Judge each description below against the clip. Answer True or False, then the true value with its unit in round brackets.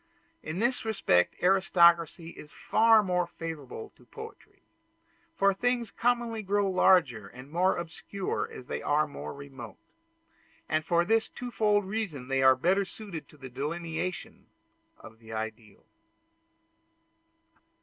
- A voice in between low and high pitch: True (175 Hz)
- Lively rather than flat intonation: True (6.6 semitones)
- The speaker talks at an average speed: False (130 wpm)